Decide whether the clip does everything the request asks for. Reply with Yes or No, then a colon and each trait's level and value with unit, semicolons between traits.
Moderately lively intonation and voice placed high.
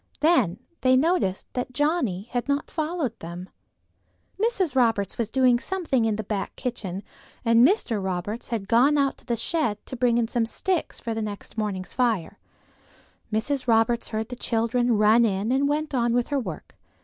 Yes: average, 4.1 semitones; high, 235 Hz